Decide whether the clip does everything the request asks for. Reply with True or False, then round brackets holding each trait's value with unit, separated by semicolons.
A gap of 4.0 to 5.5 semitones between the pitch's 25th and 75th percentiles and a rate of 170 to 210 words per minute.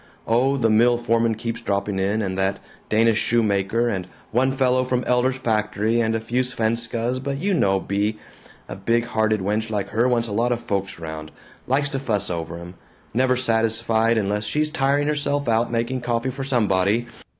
False (3.2 semitones; 185 wpm)